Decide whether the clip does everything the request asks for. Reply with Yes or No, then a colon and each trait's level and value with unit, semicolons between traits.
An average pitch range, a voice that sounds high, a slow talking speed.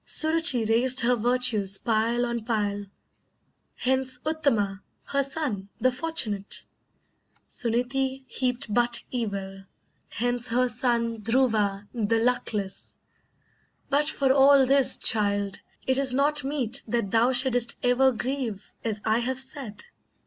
Yes: average, 3.4 semitones; high, 245 Hz; slow, 120 wpm